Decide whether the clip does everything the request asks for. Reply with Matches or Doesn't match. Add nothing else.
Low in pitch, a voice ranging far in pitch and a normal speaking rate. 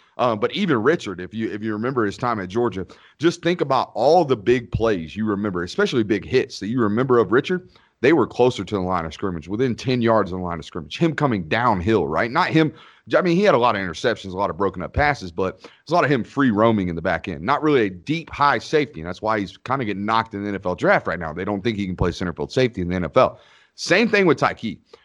Doesn't match